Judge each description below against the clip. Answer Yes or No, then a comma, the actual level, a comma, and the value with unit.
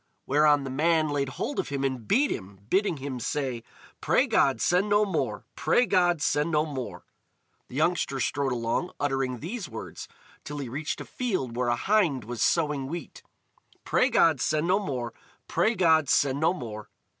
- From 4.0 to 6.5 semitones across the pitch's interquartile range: Yes, average, 4.8 semitones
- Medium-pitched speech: Yes, medium, 145 Hz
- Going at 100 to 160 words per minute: No, average, 180 wpm